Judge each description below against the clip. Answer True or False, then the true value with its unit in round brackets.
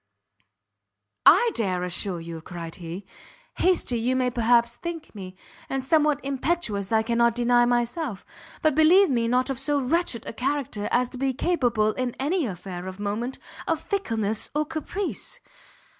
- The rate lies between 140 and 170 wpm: True (155 wpm)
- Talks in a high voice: True (245 Hz)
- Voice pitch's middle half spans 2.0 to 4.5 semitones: False (5.6 semitones)